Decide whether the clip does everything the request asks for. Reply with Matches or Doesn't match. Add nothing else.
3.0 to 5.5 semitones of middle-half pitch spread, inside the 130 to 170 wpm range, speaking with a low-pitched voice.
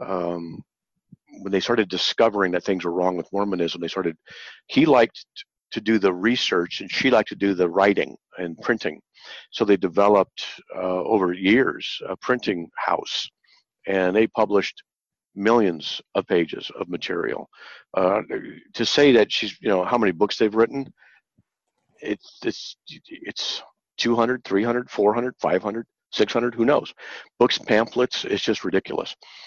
Matches